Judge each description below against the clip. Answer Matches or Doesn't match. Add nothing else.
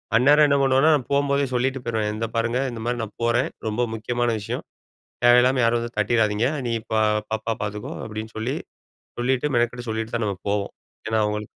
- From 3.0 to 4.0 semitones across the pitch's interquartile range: Doesn't match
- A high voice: Doesn't match